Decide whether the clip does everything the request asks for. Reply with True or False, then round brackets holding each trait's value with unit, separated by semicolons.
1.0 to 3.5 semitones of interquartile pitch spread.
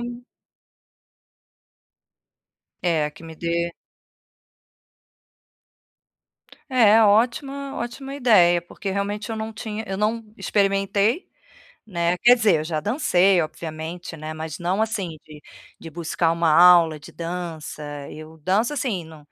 False (5.1 semitones)